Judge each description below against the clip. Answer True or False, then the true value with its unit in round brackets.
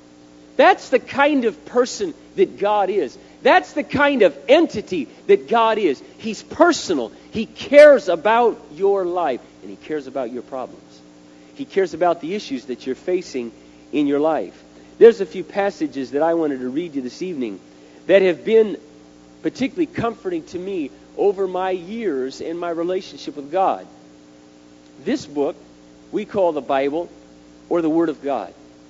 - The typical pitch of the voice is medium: True (170 Hz)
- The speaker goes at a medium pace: True (160 wpm)